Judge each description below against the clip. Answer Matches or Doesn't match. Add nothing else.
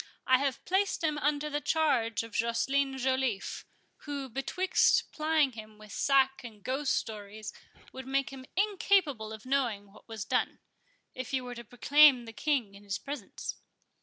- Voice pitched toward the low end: Doesn't match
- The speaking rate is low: Doesn't match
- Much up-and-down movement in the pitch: Doesn't match